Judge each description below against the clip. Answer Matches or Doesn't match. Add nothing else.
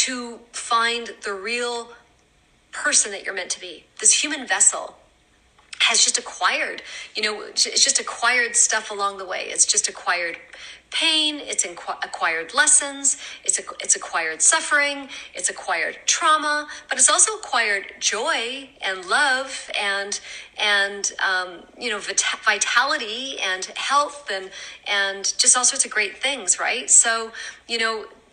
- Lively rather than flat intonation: Matches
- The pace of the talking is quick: Doesn't match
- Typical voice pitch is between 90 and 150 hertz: Doesn't match